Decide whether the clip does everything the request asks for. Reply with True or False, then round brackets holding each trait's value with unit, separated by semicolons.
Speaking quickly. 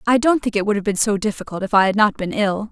True (330 wpm)